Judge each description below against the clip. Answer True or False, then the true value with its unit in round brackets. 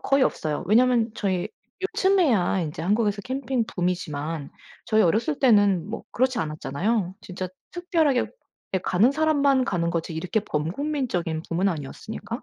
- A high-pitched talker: True (205 Hz)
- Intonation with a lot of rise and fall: True (7.2 semitones)